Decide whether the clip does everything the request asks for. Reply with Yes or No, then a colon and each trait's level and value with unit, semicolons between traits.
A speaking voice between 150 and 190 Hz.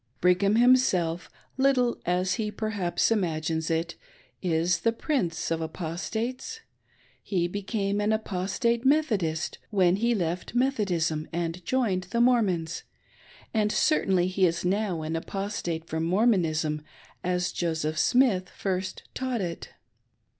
Yes: medium, 185 Hz